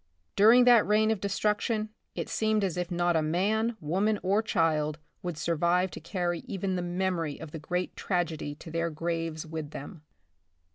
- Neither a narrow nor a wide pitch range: Yes, average, 4.2 semitones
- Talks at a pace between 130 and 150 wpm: No, average, 175 wpm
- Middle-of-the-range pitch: Yes, medium, 175 Hz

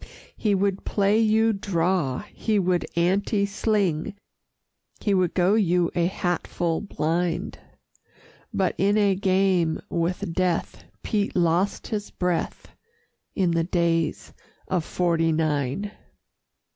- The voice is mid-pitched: Yes, medium, 180 Hz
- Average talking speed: No, slow, 115 wpm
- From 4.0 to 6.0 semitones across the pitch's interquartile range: No, average, 3.0 semitones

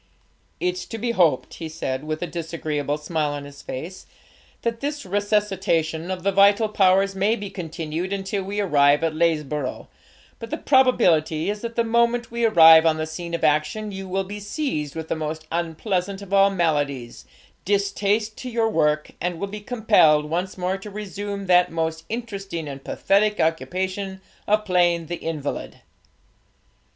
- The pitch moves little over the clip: No, average, 4.4 semitones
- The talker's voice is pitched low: No, medium, 180 Hz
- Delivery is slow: No, average, 165 wpm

